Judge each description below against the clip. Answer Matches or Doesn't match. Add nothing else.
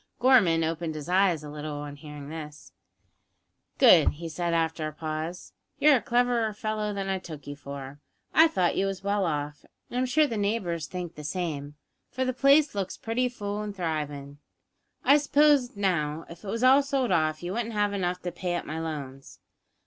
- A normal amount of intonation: Doesn't match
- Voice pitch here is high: Doesn't match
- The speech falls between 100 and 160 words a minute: Doesn't match